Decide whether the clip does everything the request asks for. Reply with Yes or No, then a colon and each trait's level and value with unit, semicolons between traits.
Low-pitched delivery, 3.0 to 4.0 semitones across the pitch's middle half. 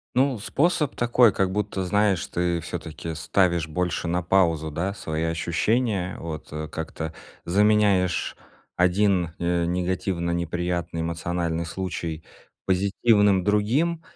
Yes: very low, 90 Hz; average, 3.5 semitones